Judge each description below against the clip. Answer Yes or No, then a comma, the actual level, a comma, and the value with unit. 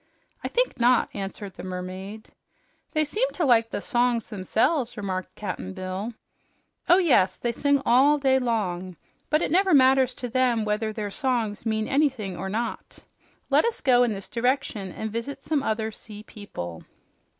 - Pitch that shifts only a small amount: No, average, 4.7 semitones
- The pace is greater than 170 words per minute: No, average, 165 wpm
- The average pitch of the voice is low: No, high, 230 Hz